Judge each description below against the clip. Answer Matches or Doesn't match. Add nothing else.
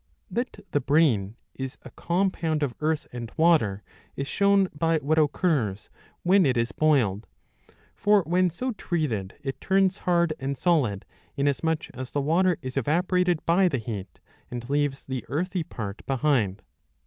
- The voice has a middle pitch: Matches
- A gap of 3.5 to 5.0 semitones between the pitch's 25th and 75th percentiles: Doesn't match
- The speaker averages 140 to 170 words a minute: Matches